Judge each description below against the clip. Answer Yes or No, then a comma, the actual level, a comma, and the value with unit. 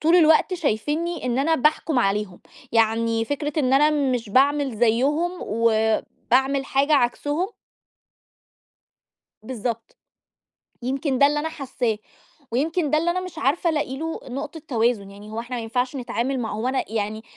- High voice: Yes, very high, 265 Hz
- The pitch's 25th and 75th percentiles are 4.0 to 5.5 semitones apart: Yes, average, 4.6 semitones